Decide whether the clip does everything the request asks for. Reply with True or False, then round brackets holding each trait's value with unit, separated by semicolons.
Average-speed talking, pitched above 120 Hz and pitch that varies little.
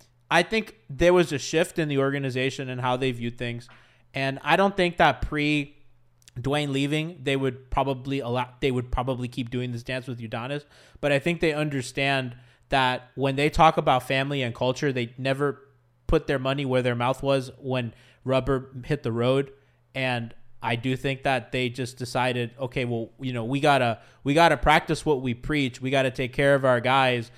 True (195 wpm; 130 Hz; 2.3 semitones)